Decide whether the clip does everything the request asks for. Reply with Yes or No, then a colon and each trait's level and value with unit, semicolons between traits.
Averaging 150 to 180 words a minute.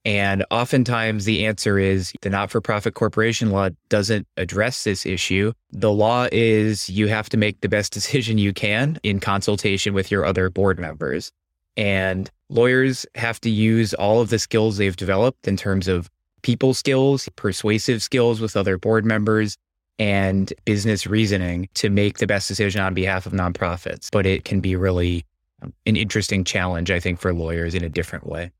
Yes: average, 175 wpm